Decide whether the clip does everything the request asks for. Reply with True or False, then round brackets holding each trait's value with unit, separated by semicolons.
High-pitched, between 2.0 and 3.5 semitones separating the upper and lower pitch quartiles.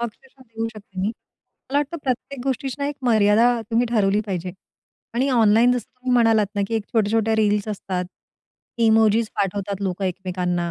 True (220 Hz; 3.2 semitones)